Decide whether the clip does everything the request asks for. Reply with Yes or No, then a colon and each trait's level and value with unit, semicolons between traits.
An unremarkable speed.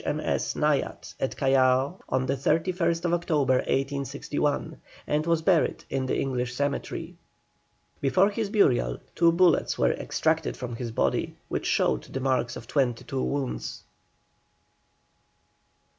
No: slow, 130 wpm